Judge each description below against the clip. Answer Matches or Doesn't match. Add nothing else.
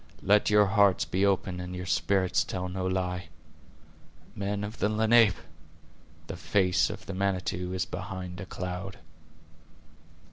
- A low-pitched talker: Matches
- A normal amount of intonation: Doesn't match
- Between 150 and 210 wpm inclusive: Doesn't match